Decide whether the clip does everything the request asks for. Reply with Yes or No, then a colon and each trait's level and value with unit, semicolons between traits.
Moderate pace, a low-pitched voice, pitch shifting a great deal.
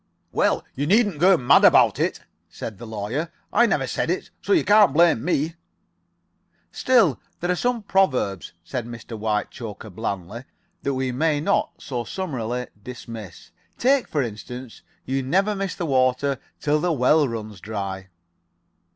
Yes: average, 150 wpm; low, 130 Hz; wide, 7.4 semitones